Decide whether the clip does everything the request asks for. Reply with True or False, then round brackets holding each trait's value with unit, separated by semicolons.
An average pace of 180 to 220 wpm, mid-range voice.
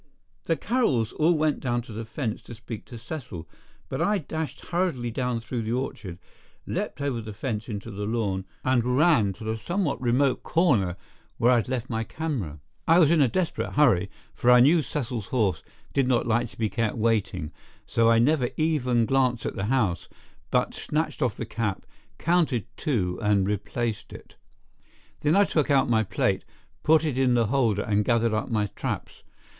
False (185 wpm; 120 Hz)